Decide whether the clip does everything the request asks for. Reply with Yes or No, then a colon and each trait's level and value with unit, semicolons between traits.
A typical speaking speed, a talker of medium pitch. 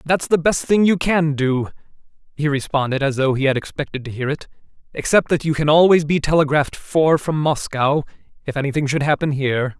Yes: average, 195 wpm; medium, 150 Hz